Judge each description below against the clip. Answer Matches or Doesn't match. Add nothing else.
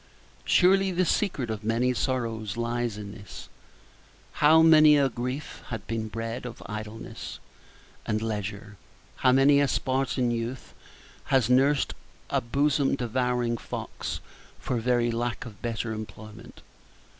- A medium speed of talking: Doesn't match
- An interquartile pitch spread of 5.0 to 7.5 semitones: Doesn't match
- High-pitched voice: Doesn't match